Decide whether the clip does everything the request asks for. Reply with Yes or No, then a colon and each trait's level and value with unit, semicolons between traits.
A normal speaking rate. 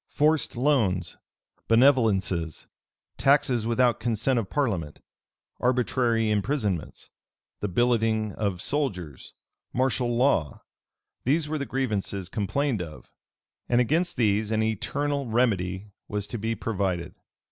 No: slow, 110 wpm